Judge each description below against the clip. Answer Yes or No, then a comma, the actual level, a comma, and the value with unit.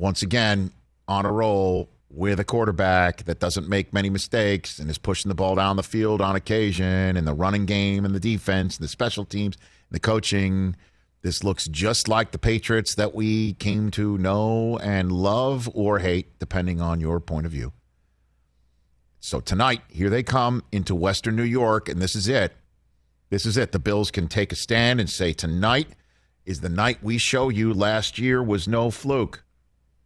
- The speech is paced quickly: No, average, 190 wpm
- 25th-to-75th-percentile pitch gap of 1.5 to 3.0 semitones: No, average, 3.6 semitones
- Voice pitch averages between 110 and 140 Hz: No, low, 100 Hz